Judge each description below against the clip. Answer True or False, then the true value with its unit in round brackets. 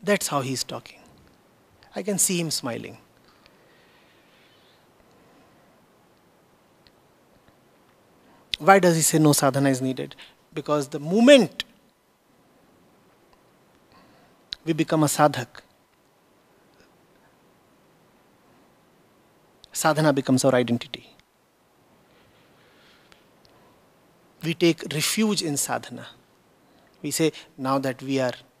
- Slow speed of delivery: True (80 wpm)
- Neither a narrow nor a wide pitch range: True (3.7 semitones)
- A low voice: False (150 Hz)